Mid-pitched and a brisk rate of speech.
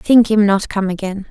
No: high, 205 Hz; fast, 230 wpm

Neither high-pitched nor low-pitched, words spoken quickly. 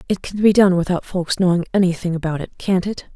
Yes: medium, 180 Hz; fast, 230 wpm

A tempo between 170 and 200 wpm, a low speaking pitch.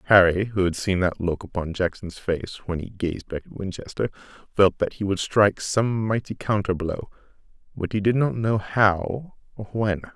Yes: average, 190 wpm; low, 100 Hz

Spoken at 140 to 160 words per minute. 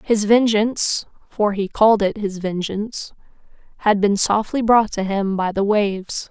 Yes: average, 145 wpm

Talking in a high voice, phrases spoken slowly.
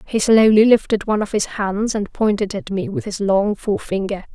No: high, 205 Hz; fast, 205 wpm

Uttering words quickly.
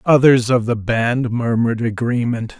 No: average, 140 wpm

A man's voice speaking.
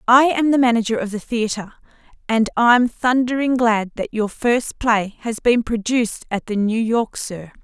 No: female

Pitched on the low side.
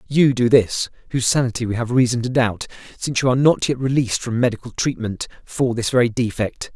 Yes: low, 120 Hz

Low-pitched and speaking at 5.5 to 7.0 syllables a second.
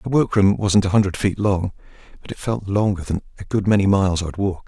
Yes: low, 100 Hz; 6.3 syllables/s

